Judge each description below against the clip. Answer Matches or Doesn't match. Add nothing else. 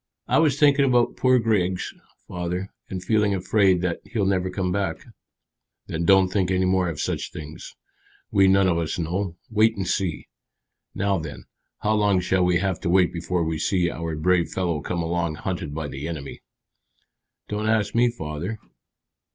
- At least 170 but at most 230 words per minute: Matches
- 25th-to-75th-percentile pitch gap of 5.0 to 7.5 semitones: Doesn't match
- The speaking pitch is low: Matches